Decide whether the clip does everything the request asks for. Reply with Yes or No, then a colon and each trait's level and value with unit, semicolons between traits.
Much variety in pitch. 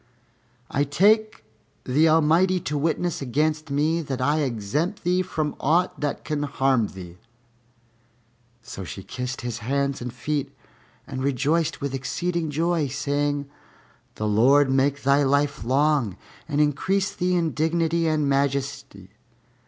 No: average, 3.2 semitones